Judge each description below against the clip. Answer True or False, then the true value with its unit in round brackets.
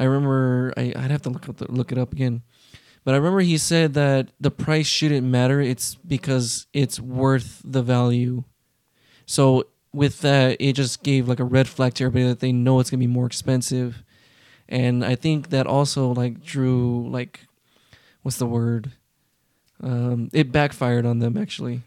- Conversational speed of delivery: True (175 wpm)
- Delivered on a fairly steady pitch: True (1.9 semitones)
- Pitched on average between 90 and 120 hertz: False (130 Hz)